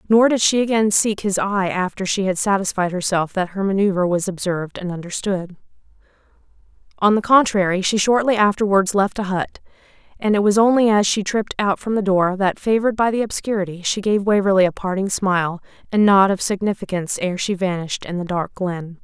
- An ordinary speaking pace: Yes, average, 190 wpm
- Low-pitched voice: No, high, 195 Hz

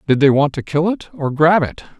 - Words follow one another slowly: No, fast, 270 wpm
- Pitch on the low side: No, medium, 155 Hz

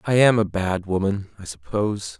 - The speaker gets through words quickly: No, average, 190 wpm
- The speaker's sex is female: No, male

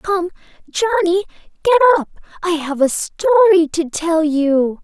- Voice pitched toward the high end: Yes, very high, 350 Hz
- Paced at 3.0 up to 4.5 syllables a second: Yes, 4.4 syllables/s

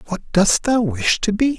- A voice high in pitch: Yes, high, 200 Hz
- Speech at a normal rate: No, fast, 225 wpm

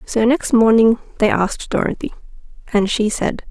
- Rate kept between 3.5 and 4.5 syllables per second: No, 5.0 syllables/s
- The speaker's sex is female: Yes, female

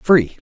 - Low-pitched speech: No, medium, 155 Hz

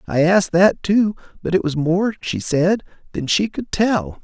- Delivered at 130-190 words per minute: No, average, 200 wpm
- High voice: No, medium, 175 Hz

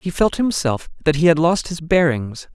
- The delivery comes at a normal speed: No, fast, 210 wpm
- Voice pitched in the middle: Yes, medium, 160 Hz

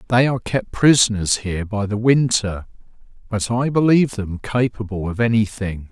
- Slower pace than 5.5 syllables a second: Yes, 5.2 syllables/s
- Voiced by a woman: No, male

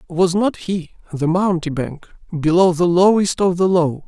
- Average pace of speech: Yes, average, 160 wpm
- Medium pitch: Yes, medium, 175 Hz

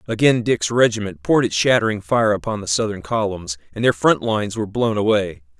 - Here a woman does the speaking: No, male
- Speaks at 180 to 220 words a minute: Yes, average, 195 wpm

